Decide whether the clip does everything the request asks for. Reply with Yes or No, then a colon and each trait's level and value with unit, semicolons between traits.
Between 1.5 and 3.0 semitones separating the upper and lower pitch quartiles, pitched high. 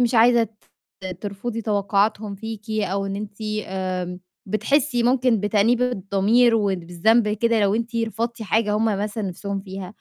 Yes: average, 2.7 semitones; high, 215 Hz